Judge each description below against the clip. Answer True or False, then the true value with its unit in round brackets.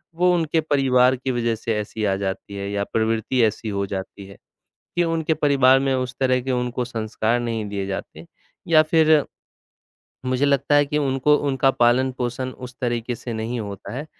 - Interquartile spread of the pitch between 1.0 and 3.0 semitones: False (3.7 semitones)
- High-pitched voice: False (125 Hz)